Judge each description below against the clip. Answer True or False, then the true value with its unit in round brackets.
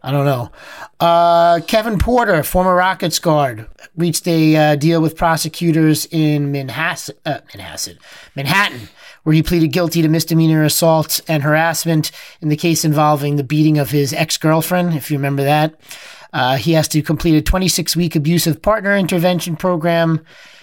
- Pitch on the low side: False (160 Hz)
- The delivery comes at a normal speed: True (155 wpm)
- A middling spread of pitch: False (1.9 semitones)